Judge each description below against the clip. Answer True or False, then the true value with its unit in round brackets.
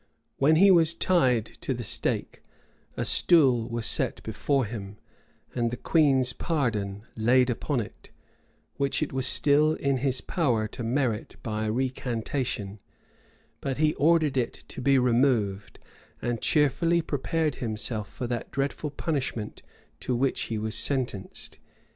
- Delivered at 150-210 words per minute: False (140 wpm)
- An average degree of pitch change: True (3.9 semitones)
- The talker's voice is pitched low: True (130 Hz)